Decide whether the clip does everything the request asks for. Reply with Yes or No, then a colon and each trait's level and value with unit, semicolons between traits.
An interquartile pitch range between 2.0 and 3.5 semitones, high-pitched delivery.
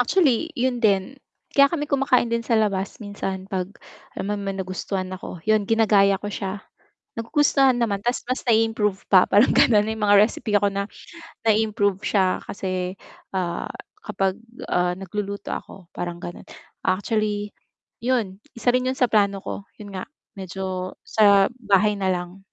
Yes: average, 2.8 semitones; high, 205 Hz